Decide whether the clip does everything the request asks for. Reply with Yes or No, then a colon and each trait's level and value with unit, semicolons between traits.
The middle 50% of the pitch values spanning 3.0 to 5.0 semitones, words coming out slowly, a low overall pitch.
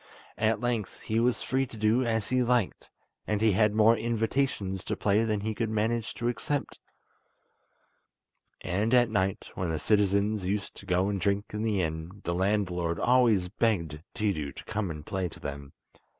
No: average, 3.4 semitones; average, 180 wpm; low, 105 Hz